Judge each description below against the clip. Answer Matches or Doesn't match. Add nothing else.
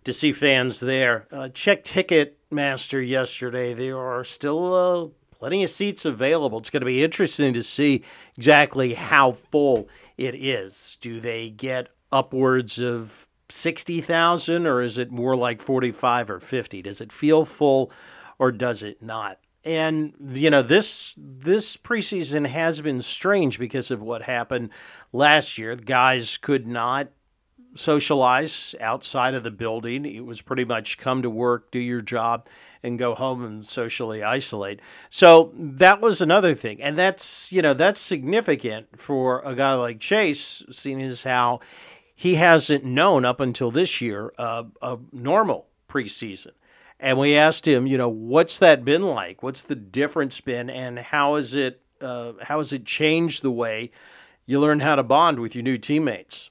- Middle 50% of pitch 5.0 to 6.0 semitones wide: Doesn't match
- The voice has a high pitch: Doesn't match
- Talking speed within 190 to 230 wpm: Doesn't match